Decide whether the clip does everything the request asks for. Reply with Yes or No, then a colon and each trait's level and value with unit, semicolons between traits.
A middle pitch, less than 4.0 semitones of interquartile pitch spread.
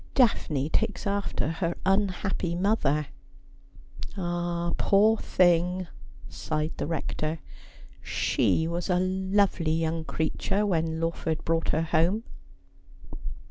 Yes: medium, 175 Hz; average, 3.1 semitones